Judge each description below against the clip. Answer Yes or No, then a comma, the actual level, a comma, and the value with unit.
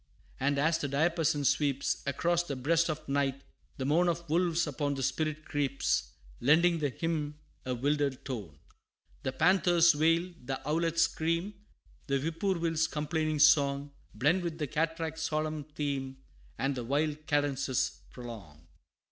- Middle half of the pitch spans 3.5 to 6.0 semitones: No, average, 2.9 semitones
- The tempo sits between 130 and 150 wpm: Yes, average, 140 wpm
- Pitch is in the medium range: Yes, medium, 150 Hz